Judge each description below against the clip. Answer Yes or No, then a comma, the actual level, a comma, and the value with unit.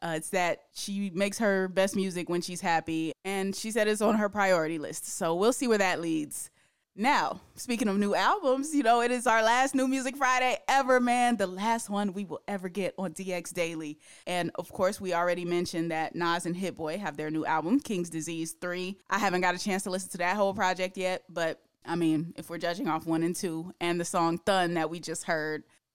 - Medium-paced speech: No, fast, 225 wpm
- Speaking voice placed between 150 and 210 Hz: Yes, medium, 185 Hz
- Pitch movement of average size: Yes, average, 3.4 semitones